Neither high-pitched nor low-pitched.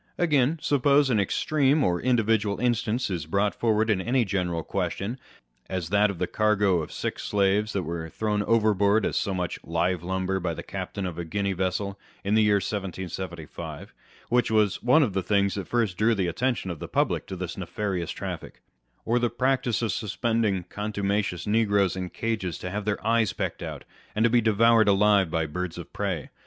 No: low, 100 Hz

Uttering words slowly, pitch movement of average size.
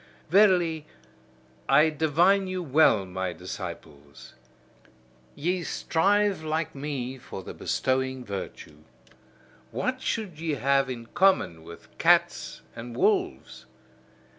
No: slow, 105 wpm; wide, 7.3 semitones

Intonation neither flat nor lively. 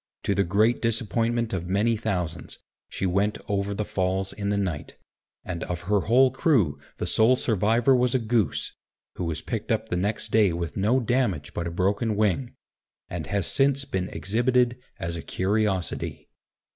Yes: average, 4.2 semitones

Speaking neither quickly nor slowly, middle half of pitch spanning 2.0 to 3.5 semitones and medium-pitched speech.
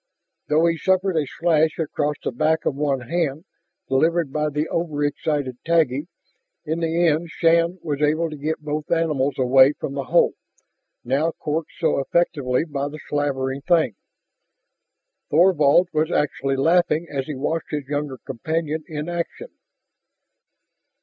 Yes: average, 145 wpm; average, 2.9 semitones; medium, 150 Hz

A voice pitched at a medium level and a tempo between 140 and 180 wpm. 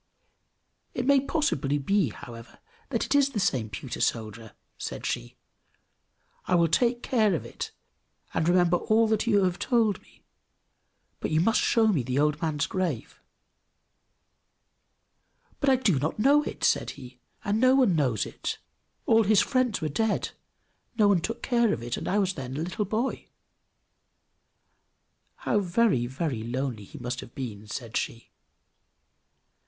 Yes: medium, 175 Hz; average, 160 wpm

